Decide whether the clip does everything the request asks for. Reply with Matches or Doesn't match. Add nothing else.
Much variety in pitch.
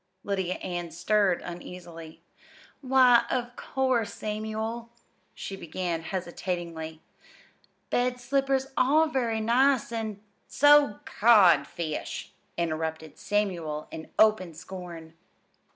Matches